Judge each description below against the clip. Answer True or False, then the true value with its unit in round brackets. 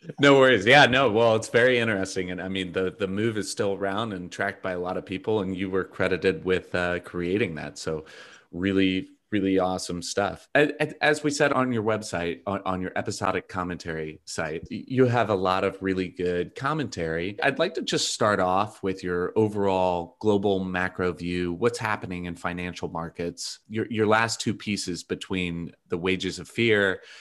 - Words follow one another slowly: False (185 wpm)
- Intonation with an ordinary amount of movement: True (3.5 semitones)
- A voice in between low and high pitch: False (95 Hz)